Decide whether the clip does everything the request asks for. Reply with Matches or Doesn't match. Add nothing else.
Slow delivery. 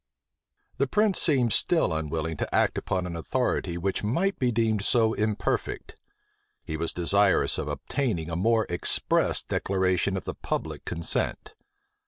Doesn't match